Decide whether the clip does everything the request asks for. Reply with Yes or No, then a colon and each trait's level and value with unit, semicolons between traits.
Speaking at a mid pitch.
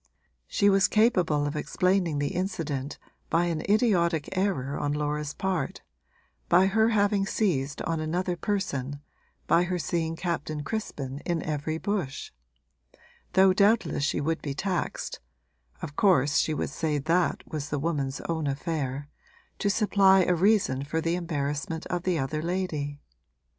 Yes: medium, 165 Hz